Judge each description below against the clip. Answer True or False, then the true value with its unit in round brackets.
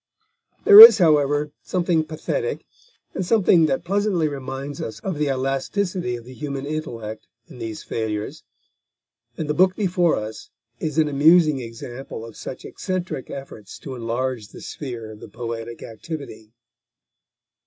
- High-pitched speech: False (140 Hz)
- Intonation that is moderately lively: False (6.2 semitones)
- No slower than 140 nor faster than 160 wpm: True (145 wpm)